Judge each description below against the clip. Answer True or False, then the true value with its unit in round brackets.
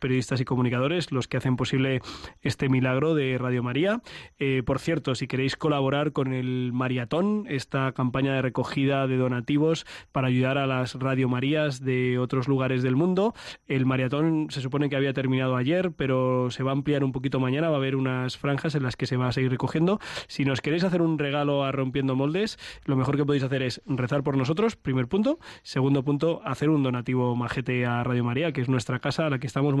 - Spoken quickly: True (210 wpm)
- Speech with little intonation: True (2.1 semitones)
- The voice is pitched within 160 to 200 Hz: False (135 Hz)